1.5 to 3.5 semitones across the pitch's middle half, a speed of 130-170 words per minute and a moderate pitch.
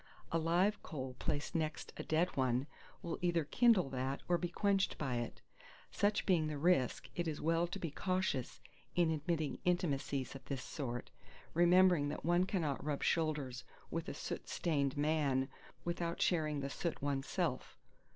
No: average, 3.9 semitones; average, 160 wpm; medium, 155 Hz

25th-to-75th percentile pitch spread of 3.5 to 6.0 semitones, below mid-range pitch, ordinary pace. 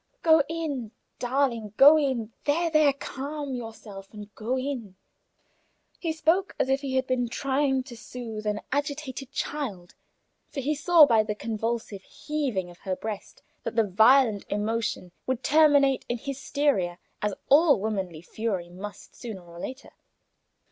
No: average, 5.2 semitones; very high, 250 Hz; average, 150 wpm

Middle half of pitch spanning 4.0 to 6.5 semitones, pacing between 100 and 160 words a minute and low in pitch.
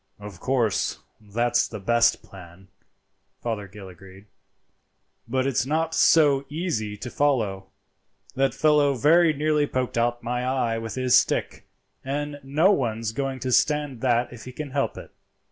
Yes: average, 4.3 semitones; average, 145 wpm; low, 125 Hz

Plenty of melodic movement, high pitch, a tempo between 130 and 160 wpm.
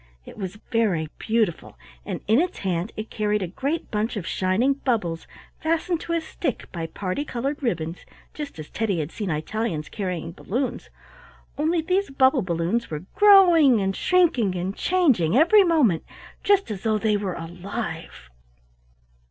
Yes: wide, 8.2 semitones; high, 215 Hz; average, 155 wpm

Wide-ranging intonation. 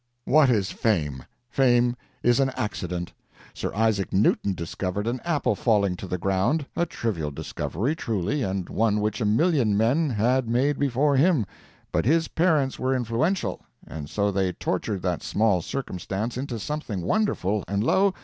Yes: wide, 5.8 semitones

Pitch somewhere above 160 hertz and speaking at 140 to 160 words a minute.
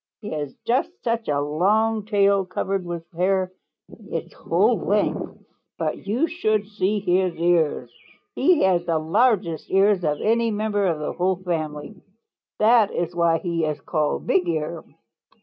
Yes: medium, 185 Hz; average, 150 wpm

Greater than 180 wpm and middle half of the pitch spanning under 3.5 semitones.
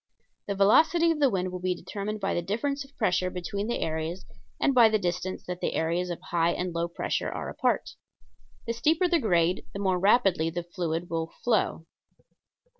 No: average, 190 wpm; average, 4.5 semitones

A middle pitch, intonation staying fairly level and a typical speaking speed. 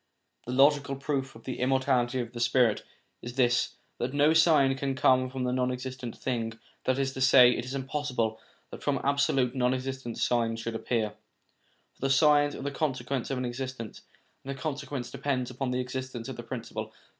No: low, 130 Hz; narrow, 2.0 semitones; average, 190 wpm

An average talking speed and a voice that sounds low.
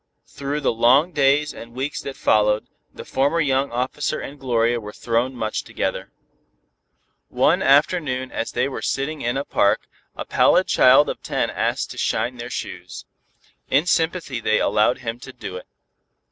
Yes: average, 165 wpm; low, 130 Hz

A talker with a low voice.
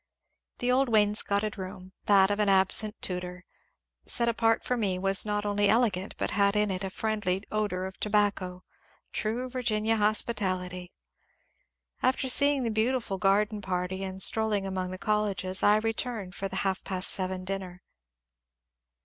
No: high, 205 Hz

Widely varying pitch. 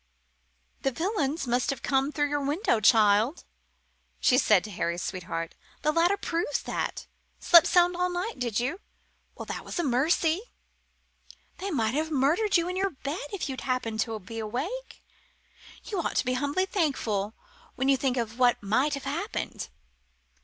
Yes: wide, 6.4 semitones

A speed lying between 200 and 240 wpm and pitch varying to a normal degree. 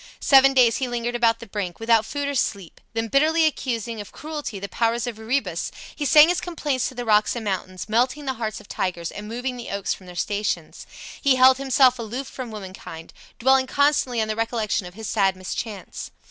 Yes: fast, 205 wpm; average, 4.0 semitones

